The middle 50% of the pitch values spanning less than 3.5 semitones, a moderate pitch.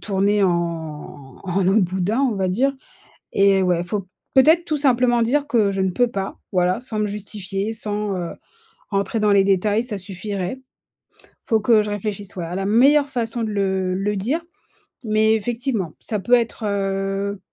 No: average, 3.1 semitones; high, 205 Hz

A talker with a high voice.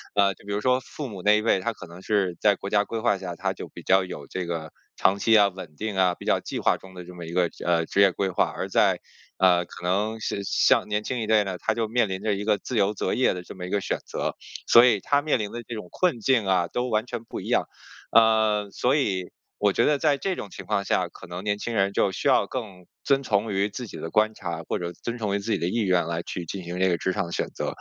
No: low, 100 Hz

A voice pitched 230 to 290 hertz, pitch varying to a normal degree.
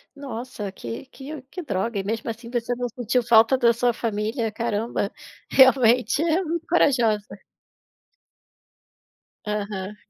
Yes: high, 235 Hz; average, 3.4 semitones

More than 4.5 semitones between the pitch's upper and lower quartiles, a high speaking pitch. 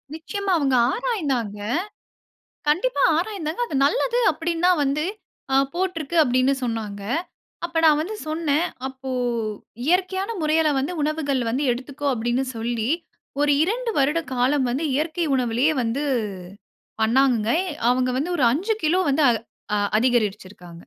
Yes: average, 5.2 semitones; very high, 290 Hz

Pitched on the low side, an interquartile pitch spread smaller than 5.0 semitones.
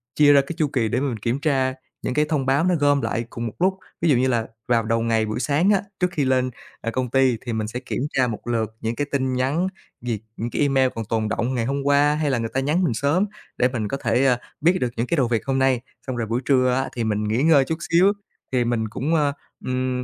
Yes: low, 130 Hz; average, 3.5 semitones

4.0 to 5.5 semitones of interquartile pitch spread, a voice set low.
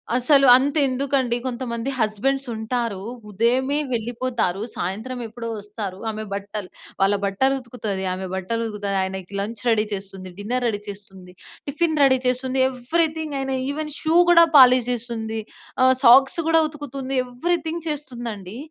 No: average, 4.4 semitones; high, 240 Hz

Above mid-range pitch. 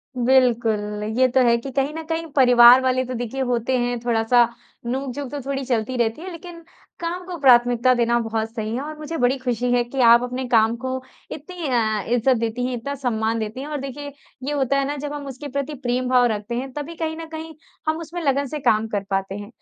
Yes: very high, 255 Hz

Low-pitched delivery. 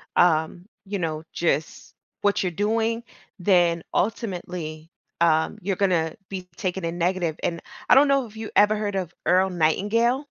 No: medium, 185 Hz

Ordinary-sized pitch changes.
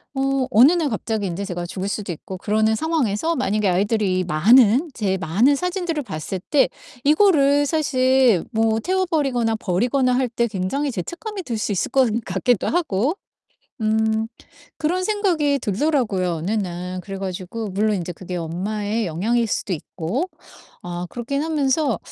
No: wide, 6.7 semitones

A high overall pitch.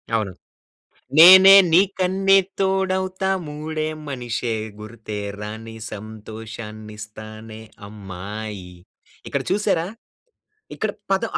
No: low, 115 Hz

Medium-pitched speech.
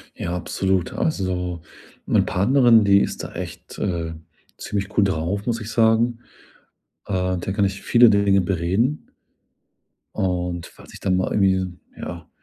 No: very low, 95 Hz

